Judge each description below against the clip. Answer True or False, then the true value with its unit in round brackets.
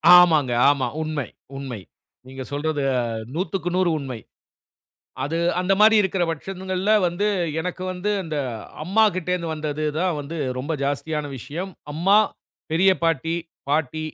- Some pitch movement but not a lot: True (3.9 semitones)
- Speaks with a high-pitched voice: False (165 Hz)